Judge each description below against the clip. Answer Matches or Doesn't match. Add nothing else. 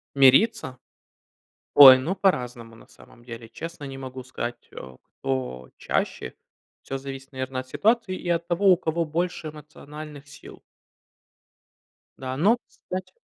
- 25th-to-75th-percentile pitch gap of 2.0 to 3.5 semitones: Doesn't match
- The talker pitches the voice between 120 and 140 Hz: Matches